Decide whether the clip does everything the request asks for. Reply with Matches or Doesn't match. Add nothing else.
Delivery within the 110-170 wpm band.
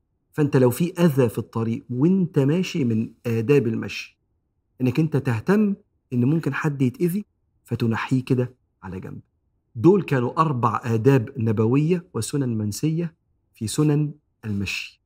Matches